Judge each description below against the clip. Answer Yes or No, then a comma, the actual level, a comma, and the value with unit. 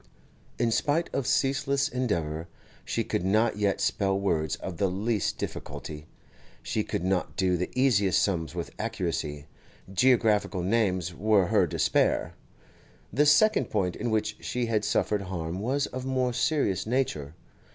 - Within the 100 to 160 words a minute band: Yes, average, 145 wpm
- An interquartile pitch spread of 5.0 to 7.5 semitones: Yes, wide, 5.5 semitones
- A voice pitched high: No, low, 105 Hz